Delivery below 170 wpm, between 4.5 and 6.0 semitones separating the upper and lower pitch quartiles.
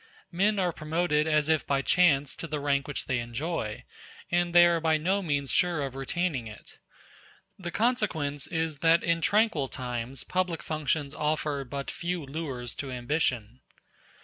No: average, 160 wpm; average, 3.9 semitones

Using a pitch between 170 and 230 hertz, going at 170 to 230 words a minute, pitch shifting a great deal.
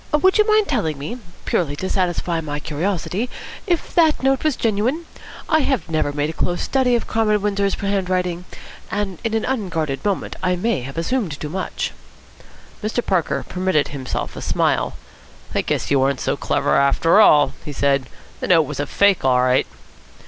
Yes: medium, 185 Hz; average, 180 wpm; wide, 7.0 semitones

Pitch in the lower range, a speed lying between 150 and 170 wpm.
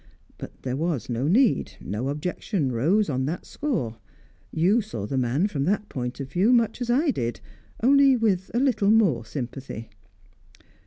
No: medium, 170 Hz; average, 165 wpm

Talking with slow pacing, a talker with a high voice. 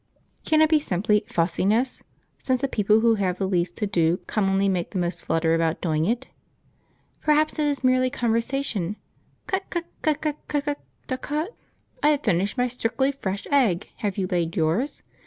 No: average, 175 wpm; high, 220 Hz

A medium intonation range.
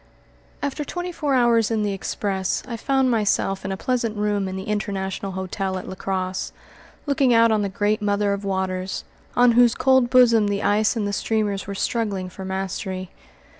Yes: average, 3.4 semitones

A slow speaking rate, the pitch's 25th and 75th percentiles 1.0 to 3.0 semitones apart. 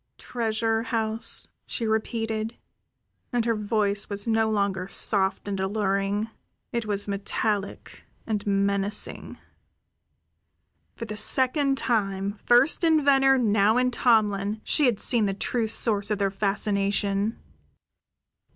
Yes: slow, 120 wpm; narrow, 2.4 semitones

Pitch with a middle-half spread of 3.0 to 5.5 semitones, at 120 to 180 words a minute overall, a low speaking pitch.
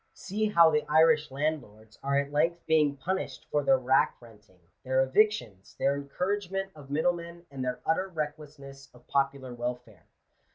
No: average, 3.9 semitones; average, 155 wpm; medium, 145 Hz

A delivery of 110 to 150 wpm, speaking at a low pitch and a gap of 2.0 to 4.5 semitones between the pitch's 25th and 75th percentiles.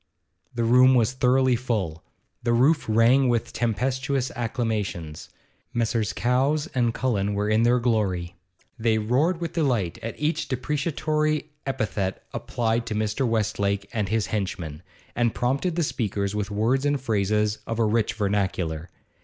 Yes: average, 145 wpm; low, 115 Hz; average, 3.9 semitones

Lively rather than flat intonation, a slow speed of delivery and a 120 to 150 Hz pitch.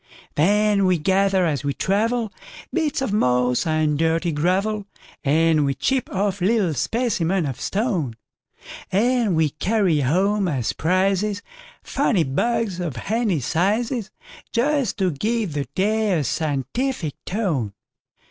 No: wide, 5.7 semitones; slow, 110 wpm; high, 190 Hz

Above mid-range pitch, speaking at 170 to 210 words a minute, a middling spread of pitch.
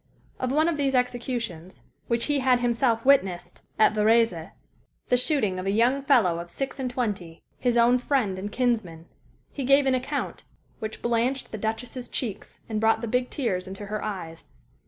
Yes: high, 235 Hz; average, 180 wpm; average, 3.9 semitones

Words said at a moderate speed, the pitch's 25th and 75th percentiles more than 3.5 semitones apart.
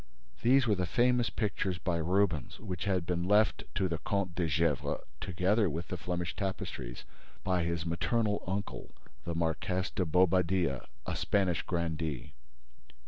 No: average, 145 wpm; average, 2.9 semitones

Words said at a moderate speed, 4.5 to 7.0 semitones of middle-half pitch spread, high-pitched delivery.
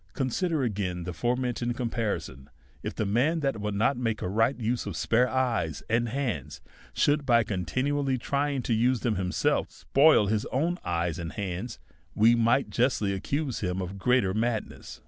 No: average, 170 wpm; average, 4.8 semitones; low, 115 Hz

